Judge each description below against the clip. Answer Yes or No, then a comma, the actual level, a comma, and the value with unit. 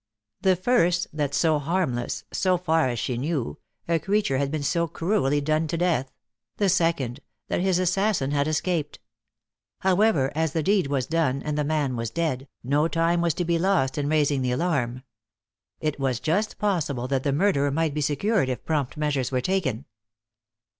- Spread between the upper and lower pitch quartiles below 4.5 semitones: Yes, average, 4.1 semitones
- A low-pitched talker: No, medium, 155 Hz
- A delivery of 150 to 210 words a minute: Yes, average, 180 wpm